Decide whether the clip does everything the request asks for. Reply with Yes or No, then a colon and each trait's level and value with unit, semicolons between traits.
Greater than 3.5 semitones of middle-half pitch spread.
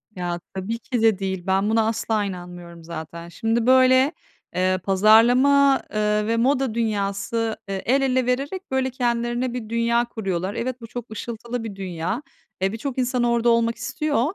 Yes: average, 4.2 semitones